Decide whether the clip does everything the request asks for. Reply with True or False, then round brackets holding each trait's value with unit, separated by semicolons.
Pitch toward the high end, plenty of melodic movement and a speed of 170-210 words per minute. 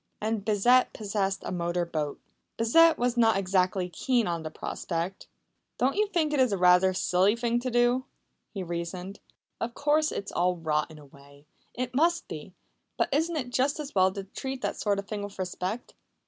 True (205 Hz; 5.9 semitones; 190 wpm)